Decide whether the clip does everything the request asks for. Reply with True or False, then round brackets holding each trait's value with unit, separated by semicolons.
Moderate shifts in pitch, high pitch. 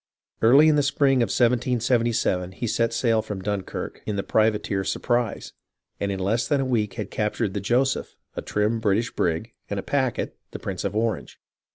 False (3.2 semitones; 115 Hz)